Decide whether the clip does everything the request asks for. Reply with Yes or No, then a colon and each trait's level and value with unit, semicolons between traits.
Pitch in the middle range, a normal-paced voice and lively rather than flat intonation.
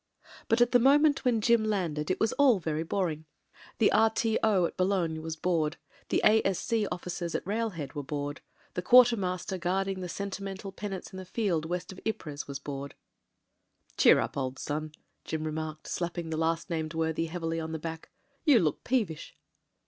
No: medium, 180 Hz; average, 175 wpm; average, 4.7 semitones